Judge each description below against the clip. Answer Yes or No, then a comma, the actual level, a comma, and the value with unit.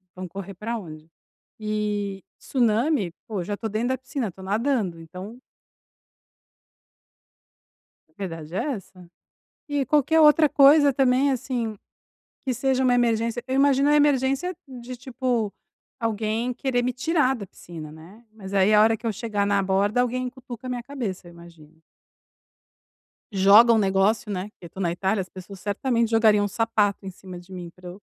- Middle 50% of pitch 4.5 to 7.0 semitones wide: Yes, average, 4.8 semitones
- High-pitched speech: Yes, high, 220 Hz